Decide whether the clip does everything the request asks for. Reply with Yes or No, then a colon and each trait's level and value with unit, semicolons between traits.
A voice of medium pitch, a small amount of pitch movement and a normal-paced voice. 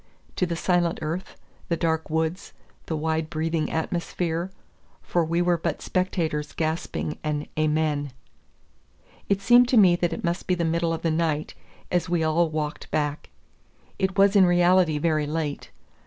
Yes: medium, 165 Hz; narrow, 2.1 semitones; average, 165 wpm